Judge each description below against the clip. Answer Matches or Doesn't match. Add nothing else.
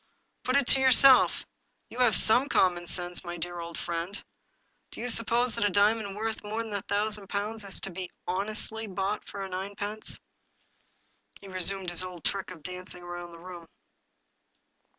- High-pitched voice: Matches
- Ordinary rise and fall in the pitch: Matches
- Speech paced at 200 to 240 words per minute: Doesn't match